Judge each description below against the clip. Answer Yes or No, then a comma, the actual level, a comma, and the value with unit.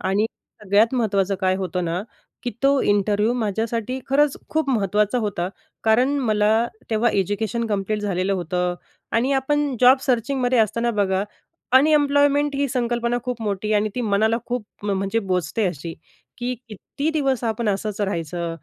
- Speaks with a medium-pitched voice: No, high, 220 Hz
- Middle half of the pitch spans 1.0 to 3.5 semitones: No, average, 4.2 semitones